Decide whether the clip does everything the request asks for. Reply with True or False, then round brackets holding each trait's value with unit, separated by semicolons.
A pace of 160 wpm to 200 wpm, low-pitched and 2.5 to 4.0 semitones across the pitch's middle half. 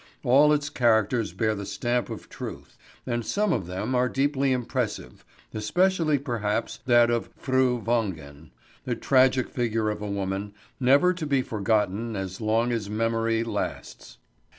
False (150 wpm; 115 Hz; 3.6 semitones)